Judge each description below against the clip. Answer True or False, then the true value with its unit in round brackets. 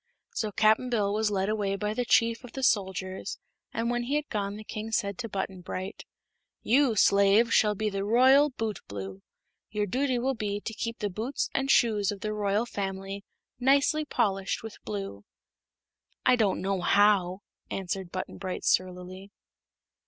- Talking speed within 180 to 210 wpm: False (165 wpm)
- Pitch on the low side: False (210 Hz)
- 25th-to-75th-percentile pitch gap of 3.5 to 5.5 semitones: False (3.1 semitones)